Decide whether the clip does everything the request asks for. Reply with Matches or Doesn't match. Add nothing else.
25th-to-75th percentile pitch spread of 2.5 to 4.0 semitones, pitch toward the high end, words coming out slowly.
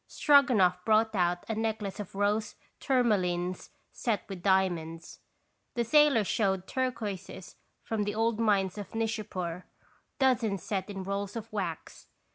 Matches